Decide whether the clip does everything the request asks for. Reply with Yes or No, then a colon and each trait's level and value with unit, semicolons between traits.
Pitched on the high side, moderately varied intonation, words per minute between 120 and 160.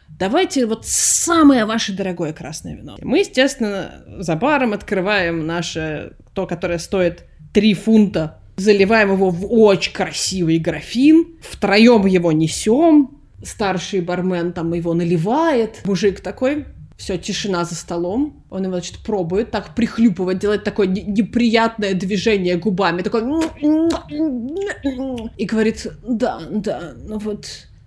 Yes: high, 205 Hz; average, 4.3 semitones; average, 125 wpm